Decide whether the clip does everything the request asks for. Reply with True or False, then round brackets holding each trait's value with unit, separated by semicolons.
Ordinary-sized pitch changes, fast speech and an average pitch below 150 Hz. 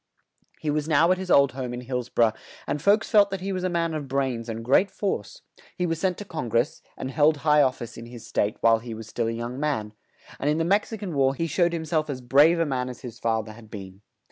False (6.0 semitones; 275 wpm; 140 Hz)